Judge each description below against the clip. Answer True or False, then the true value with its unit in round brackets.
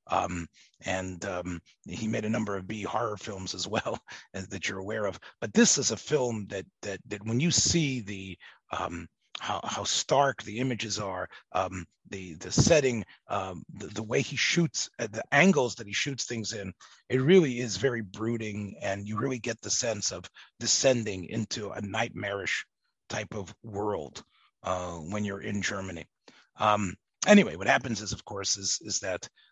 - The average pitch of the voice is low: True (105 Hz)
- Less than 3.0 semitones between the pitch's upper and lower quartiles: False (3.6 semitones)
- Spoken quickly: False (180 wpm)